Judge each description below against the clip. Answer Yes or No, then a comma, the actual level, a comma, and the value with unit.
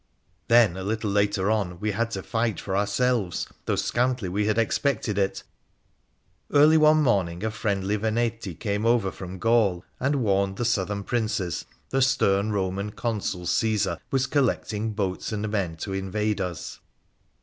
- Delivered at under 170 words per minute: Yes, average, 155 wpm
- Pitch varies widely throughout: No, average, 3.1 semitones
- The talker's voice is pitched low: Yes, low, 105 Hz